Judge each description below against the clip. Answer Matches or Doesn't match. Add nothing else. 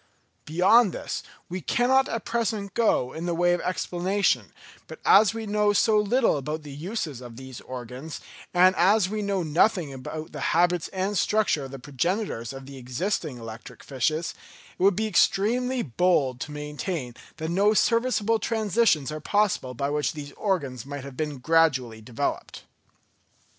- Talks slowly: Doesn't match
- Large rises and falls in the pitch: Matches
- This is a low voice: Doesn't match